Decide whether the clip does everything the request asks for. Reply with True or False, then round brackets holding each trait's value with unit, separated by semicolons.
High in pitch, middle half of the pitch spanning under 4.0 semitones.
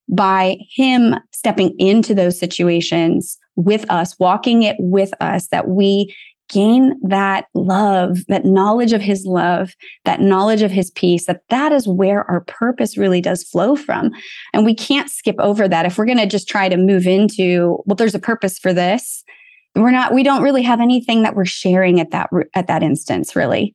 True (195 Hz; 3.6 semitones)